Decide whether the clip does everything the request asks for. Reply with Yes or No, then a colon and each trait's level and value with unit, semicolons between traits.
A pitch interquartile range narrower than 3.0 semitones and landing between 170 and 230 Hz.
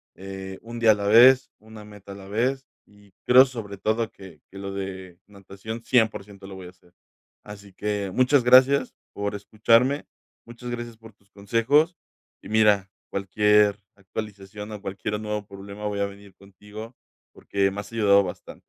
No: narrow, 2.5 semitones; low, 105 Hz